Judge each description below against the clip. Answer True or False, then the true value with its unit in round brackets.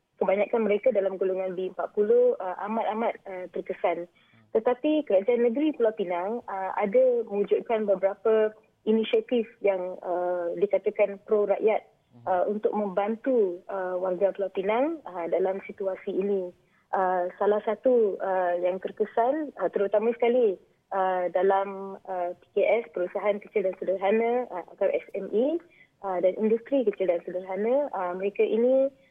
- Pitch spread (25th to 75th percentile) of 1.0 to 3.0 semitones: False (3.5 semitones)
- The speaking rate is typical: True (130 wpm)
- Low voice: False (200 Hz)